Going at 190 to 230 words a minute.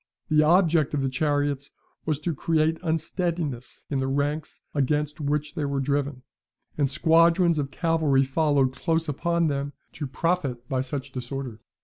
No: average, 150 wpm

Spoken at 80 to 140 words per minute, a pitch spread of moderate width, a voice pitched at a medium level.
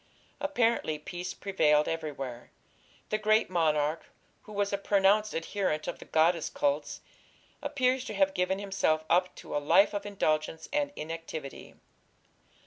Yes: slow, 135 wpm; average, 4.7 semitones; medium, 180 Hz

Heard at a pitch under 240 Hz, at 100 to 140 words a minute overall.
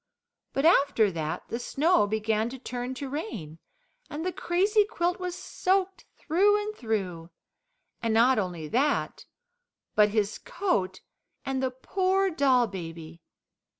No: very high, 260 Hz; slow, 135 wpm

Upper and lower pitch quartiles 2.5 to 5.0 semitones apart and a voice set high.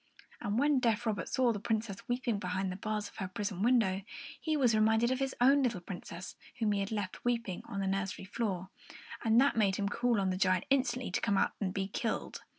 Yes: average, 3.8 semitones; high, 215 Hz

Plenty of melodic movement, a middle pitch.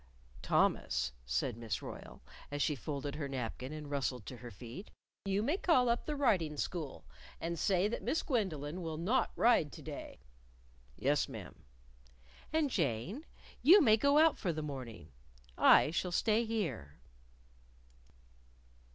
Yes: wide, 8.8 semitones; medium, 165 Hz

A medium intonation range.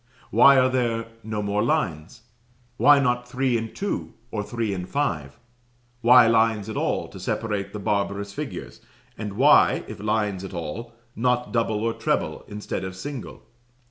Yes: average, 3.3 semitones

